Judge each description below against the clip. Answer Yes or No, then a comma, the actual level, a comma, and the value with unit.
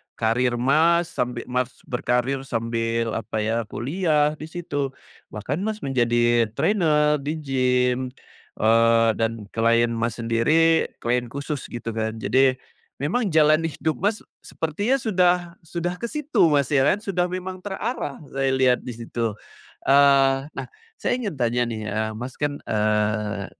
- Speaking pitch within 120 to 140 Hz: Yes, low, 135 Hz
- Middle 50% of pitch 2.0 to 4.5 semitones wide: No, wide, 5.5 semitones